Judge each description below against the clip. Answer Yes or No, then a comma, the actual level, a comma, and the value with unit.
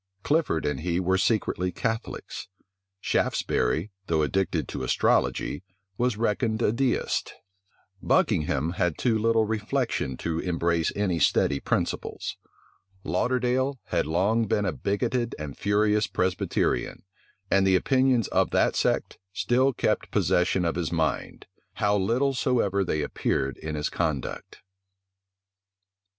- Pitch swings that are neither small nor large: No, wide, 5.7 semitones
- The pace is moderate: No, slow, 125 wpm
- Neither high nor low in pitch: No, low, 100 Hz